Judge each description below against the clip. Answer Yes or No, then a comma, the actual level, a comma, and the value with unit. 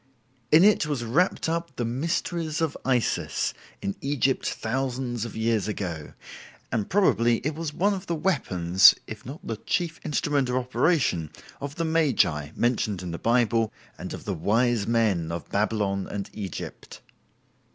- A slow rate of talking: No, average, 155 wpm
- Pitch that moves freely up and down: Yes, wide, 6.6 semitones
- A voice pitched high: No, low, 120 Hz